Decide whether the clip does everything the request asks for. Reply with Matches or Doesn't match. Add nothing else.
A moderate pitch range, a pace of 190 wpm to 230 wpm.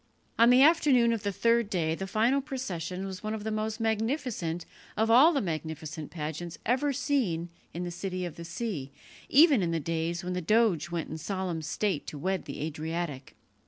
Doesn't match